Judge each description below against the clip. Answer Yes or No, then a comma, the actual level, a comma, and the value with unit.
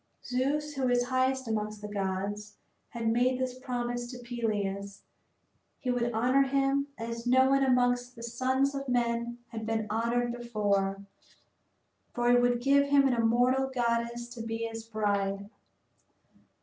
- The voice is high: Yes, high, 240 Hz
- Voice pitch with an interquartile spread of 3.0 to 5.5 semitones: No, narrow, 2.4 semitones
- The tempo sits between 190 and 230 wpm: No, average, 150 wpm